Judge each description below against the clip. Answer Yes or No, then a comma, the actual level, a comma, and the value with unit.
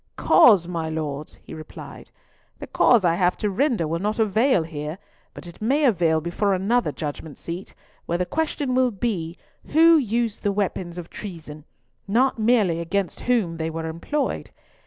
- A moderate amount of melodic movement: No, wide, 6.0 semitones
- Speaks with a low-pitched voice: No, medium, 185 Hz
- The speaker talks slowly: No, average, 165 wpm